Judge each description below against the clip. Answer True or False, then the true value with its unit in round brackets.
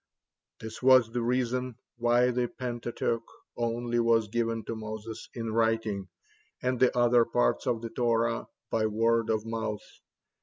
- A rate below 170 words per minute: True (150 wpm)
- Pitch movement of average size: False (1.3 semitones)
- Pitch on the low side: True (115 Hz)